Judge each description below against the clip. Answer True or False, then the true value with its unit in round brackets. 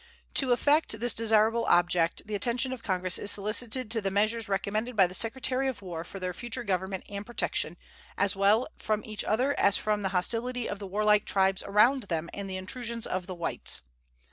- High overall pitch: True (210 Hz)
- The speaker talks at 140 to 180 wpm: False (195 wpm)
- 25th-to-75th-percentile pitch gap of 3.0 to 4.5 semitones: True (3.4 semitones)